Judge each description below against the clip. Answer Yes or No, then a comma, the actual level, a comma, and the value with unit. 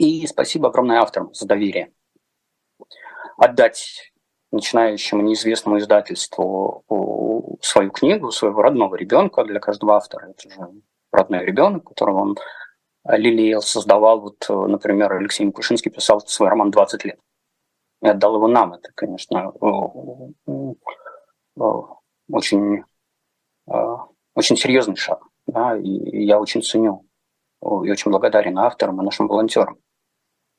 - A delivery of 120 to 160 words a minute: No, slow, 110 wpm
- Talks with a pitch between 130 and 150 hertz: No, low, 105 Hz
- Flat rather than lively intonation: Yes, narrow, 1.3 semitones